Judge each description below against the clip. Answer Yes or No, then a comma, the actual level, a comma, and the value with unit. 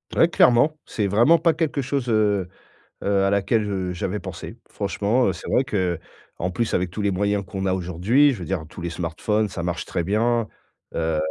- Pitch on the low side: Yes, low, 100 Hz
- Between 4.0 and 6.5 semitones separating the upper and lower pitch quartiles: Yes, average, 4.5 semitones